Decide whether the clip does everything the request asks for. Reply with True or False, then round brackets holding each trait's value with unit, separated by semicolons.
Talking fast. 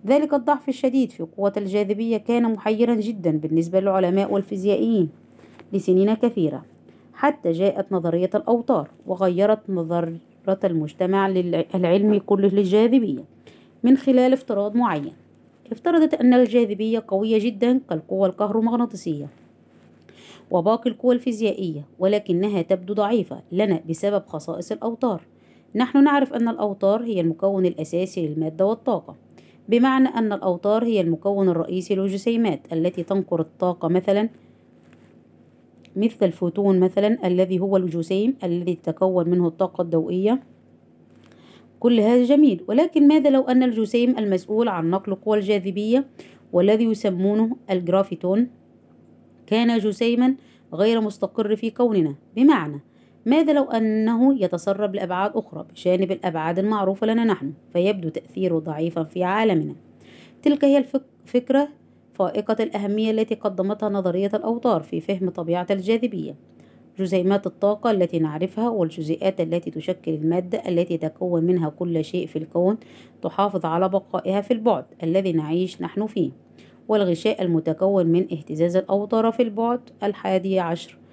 False (120 wpm)